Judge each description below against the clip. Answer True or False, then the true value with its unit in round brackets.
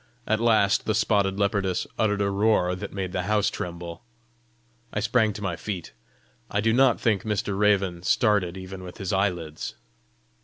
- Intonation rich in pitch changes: False (2.5 semitones)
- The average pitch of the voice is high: False (100 Hz)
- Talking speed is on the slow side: False (165 wpm)